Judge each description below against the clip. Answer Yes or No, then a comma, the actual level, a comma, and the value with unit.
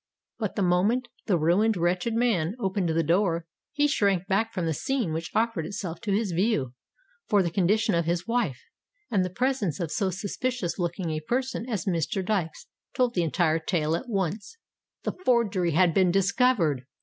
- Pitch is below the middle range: No, high, 190 Hz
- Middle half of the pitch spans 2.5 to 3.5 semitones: No, average, 4.8 semitones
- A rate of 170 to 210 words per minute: Yes, average, 175 wpm